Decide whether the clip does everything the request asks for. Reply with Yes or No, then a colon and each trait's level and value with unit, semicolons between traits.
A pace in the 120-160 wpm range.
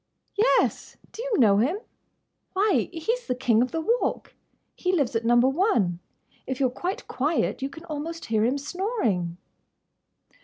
Yes: average, 155 wpm